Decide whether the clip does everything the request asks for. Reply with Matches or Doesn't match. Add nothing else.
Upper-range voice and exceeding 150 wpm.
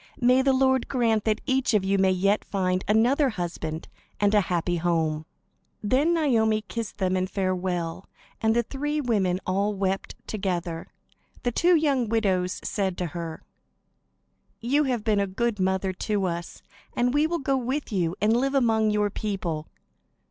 Matches